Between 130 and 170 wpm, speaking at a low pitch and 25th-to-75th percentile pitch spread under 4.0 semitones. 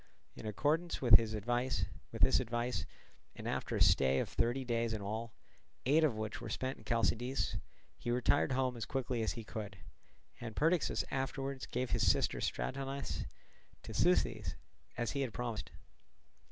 Yes: average, 155 wpm; low, 120 Hz; average, 3.2 semitones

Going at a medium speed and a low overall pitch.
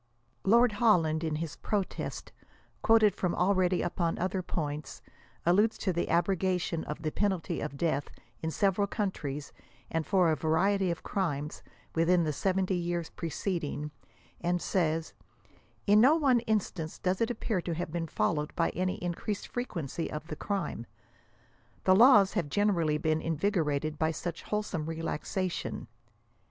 No: average, 155 wpm; medium, 175 Hz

